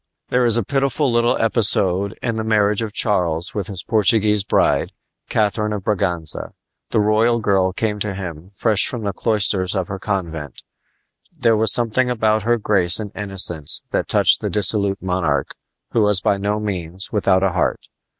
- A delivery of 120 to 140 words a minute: No, average, 170 wpm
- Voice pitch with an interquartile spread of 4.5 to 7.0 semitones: No, average, 2.9 semitones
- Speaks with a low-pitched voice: Yes, low, 105 Hz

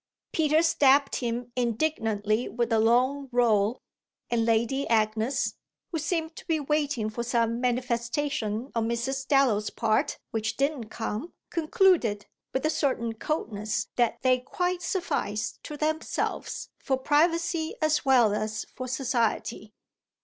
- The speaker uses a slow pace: Yes, slow, 130 wpm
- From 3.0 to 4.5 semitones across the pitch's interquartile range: No, average, 4.9 semitones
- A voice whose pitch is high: Yes, very high, 250 Hz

